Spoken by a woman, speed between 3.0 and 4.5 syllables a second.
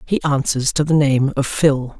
Yes: female; 4.4 syllables/s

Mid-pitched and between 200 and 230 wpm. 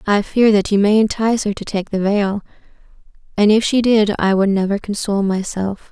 No: high, 205 Hz; fast, 205 wpm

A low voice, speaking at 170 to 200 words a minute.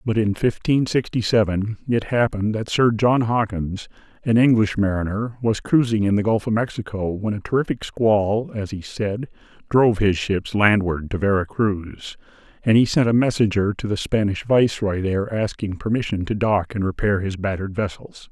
Yes: low, 105 Hz; average, 175 wpm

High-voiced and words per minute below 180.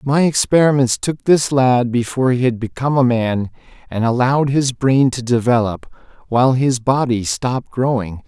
No: low, 125 Hz; average, 160 wpm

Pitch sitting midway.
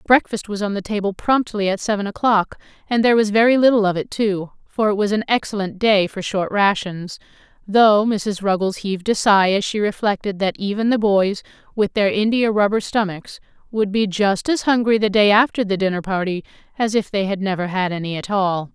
No: high, 205 Hz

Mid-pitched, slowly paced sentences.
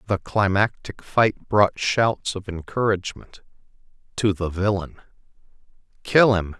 No: low, 100 Hz; slow, 100 wpm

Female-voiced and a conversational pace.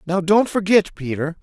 No: male; average, 170 wpm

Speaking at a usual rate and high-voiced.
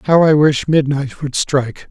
No: average, 190 wpm; medium, 145 Hz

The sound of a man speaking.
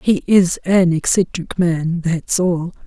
No: female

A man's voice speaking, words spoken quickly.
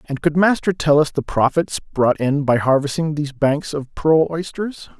No: male; average, 190 wpm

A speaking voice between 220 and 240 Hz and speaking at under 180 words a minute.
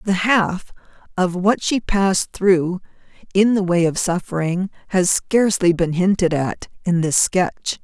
No: medium, 185 Hz; average, 155 wpm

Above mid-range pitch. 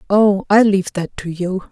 Yes: high, 195 Hz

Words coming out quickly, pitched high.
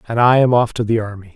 No: fast, 310 wpm; low, 115 Hz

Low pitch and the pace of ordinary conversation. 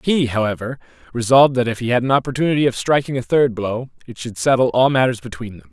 No: low, 125 Hz; fast, 220 wpm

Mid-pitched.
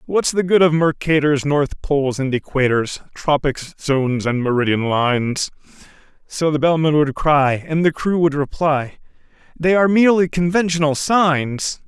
Yes: medium, 150 Hz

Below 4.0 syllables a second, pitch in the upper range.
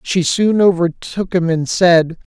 No: 3.8 syllables/s; medium, 175 Hz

